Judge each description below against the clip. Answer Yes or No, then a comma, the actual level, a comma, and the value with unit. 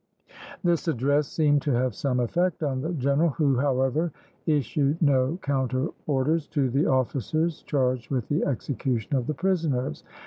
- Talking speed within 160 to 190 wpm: No, average, 150 wpm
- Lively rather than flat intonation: No, average, 3.2 semitones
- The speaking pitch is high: No, medium, 140 Hz